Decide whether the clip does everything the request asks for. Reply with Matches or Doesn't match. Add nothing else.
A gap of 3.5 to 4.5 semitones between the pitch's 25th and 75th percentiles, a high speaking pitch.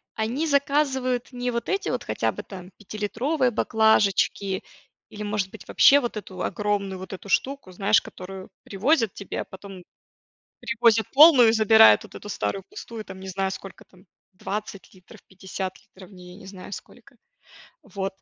Matches